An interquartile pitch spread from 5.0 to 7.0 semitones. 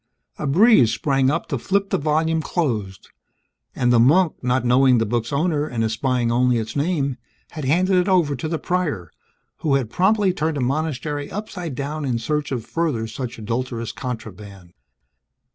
Yes: average, 5.3 semitones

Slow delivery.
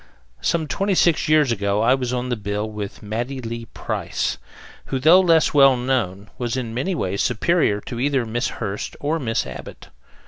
No: average, 180 wpm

